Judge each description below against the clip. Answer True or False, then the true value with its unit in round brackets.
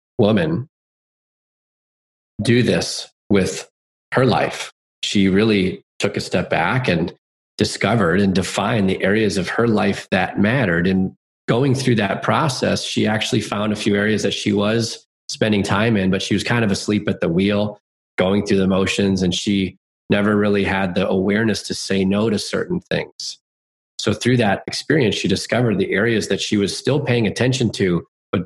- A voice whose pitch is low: True (100 Hz)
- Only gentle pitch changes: True (2.3 semitones)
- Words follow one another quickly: False (170 wpm)